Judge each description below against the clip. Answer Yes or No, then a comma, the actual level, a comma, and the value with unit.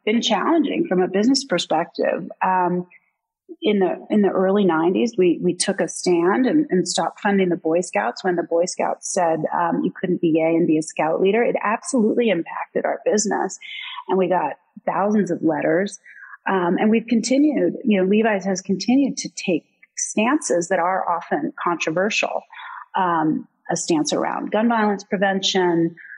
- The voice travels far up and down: Yes, wide, 6.5 semitones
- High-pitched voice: Yes, high, 200 Hz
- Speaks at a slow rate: No, average, 170 wpm